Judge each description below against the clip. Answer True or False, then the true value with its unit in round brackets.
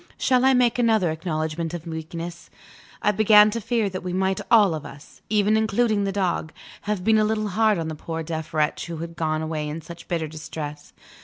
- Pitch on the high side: False (175 Hz)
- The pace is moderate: False (210 wpm)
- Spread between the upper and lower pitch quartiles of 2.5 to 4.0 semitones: False (5.0 semitones)